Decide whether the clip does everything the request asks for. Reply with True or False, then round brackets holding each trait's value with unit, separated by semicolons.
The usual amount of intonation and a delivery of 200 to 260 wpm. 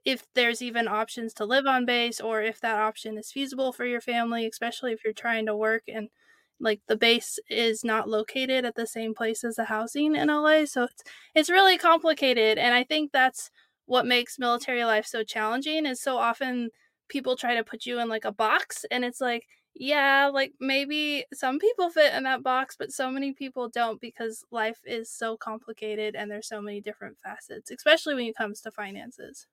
True (3.2 semitones; 205 wpm)